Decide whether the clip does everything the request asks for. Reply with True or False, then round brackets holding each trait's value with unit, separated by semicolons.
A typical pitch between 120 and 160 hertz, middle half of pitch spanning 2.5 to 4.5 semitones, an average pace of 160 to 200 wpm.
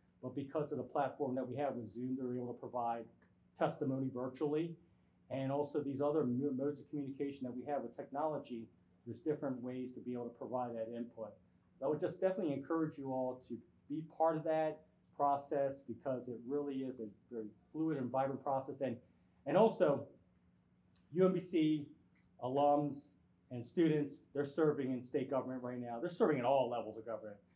True (135 Hz; 3.1 semitones; 185 wpm)